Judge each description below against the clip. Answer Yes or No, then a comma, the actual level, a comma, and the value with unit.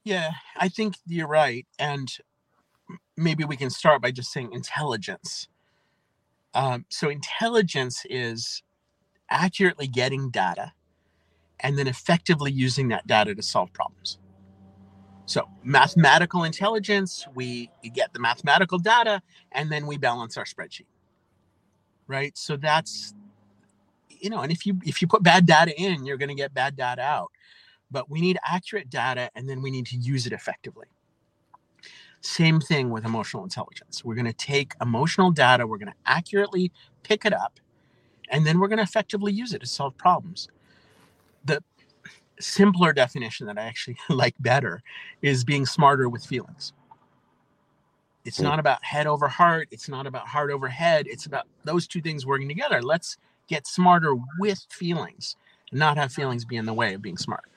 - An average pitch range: No, wide, 5.9 semitones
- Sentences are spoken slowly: No, average, 160 wpm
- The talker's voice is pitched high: No, medium, 140 Hz